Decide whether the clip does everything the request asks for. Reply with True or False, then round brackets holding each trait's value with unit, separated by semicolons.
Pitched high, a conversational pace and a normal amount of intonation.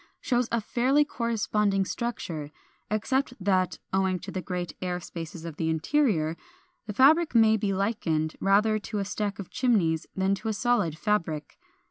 True (200 Hz; 165 wpm; 4.7 semitones)